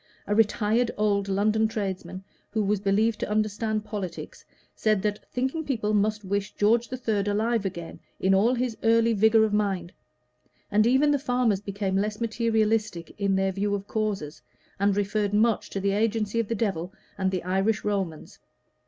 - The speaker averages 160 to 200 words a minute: Yes, average, 170 wpm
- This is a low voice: No, high, 210 Hz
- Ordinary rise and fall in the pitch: No, narrow, 2.1 semitones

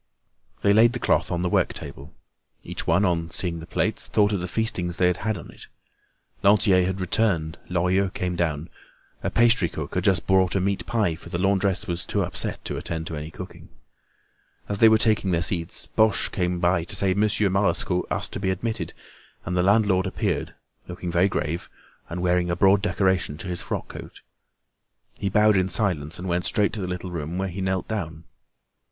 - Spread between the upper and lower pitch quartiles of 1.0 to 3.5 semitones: Yes, narrow, 2.6 semitones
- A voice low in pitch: Yes, very low, 95 Hz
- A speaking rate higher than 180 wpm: Yes, average, 200 wpm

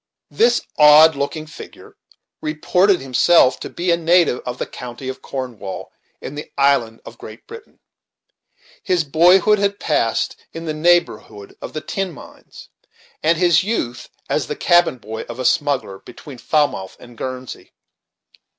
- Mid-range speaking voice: Yes, medium, 150 Hz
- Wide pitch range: Yes, wide, 5.7 semitones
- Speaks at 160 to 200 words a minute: No, average, 150 wpm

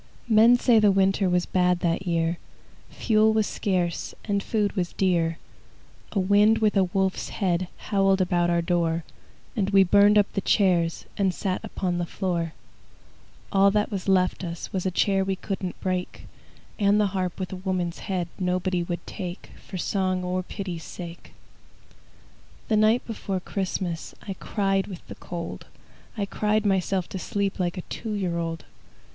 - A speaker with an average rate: Yes, average, 165 wpm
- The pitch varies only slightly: Yes, narrow, 2.2 semitones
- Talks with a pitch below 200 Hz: Yes, high, 190 Hz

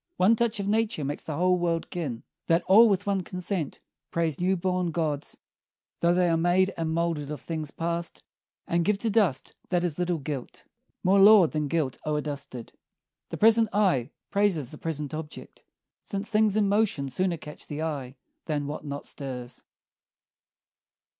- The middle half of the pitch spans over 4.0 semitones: Yes, average, 4.5 semitones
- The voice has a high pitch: No, medium, 170 Hz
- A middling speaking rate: Yes, average, 175 wpm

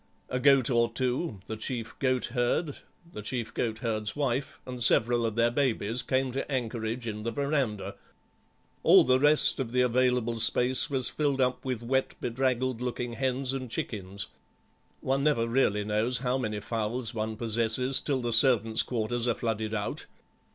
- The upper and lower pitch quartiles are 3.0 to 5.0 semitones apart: No, narrow, 2.5 semitones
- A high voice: No, low, 120 Hz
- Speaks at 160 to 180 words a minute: Yes, average, 165 wpm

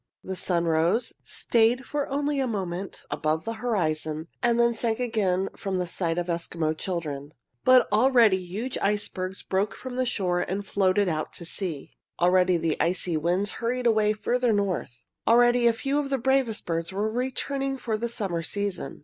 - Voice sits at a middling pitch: No, high, 200 Hz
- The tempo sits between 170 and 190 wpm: Yes, average, 175 wpm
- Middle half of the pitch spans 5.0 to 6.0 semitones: Yes, wide, 5.5 semitones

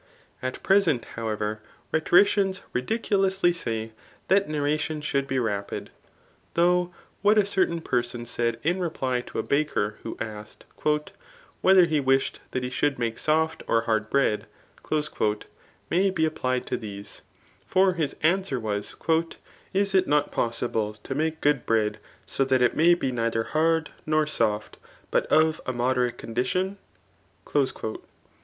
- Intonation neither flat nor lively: No, wide, 6.4 semitones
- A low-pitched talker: No, medium, 145 Hz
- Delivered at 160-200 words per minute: No, average, 145 wpm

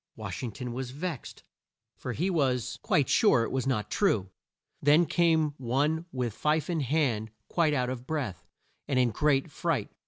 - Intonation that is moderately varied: Yes, average, 4.1 semitones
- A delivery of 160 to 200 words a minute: Yes, average, 180 wpm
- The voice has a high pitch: No, low, 135 Hz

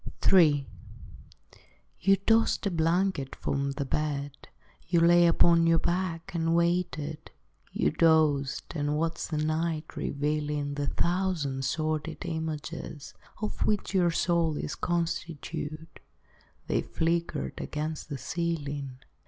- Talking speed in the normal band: No, slow, 115 wpm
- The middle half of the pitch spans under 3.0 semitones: Yes, narrow, 2.6 semitones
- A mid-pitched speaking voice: Yes, medium, 160 Hz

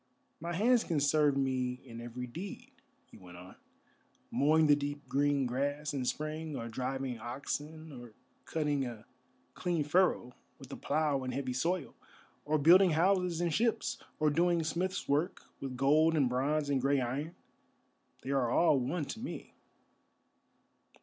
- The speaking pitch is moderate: Yes, medium, 145 Hz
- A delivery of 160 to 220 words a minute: No, average, 150 wpm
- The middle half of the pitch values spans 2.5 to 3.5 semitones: No, average, 3.9 semitones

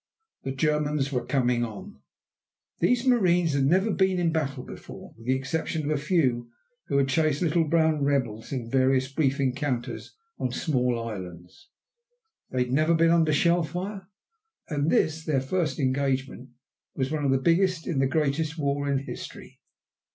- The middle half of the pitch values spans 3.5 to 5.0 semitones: Yes, average, 3.8 semitones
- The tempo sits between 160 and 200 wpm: Yes, average, 165 wpm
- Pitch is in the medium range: Yes, medium, 145 Hz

